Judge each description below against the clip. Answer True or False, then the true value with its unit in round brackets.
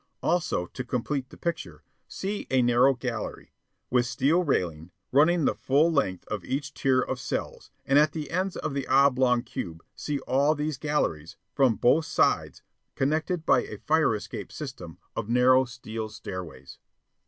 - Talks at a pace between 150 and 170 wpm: True (160 wpm)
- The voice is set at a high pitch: False (130 Hz)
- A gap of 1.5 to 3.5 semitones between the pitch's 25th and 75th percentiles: False (4.1 semitones)